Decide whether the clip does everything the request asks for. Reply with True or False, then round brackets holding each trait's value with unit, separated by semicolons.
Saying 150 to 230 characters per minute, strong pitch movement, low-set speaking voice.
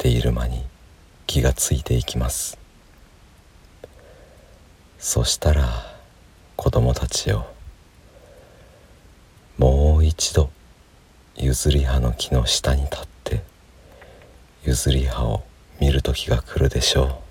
False (185 characters per minute; 3.8 semitones; 70 Hz)